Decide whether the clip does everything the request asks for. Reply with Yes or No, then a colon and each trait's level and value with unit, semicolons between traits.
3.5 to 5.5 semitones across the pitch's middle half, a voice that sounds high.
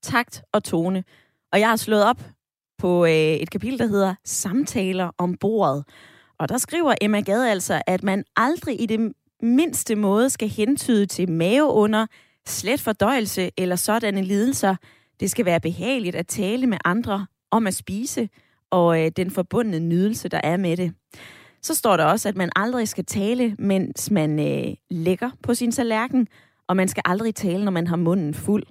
Yes: average, 4.1 semitones; high, 200 Hz